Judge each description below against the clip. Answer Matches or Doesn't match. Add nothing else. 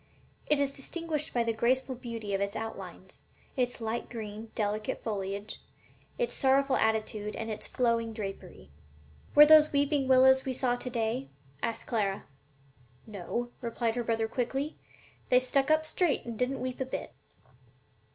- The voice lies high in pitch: Matches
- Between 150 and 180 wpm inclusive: Matches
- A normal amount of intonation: Matches